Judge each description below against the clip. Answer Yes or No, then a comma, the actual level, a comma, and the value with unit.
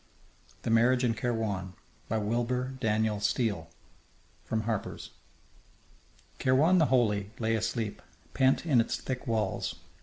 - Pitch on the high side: No, low, 115 Hz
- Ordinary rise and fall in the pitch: Yes, average, 3.1 semitones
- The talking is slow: Yes, slow, 120 wpm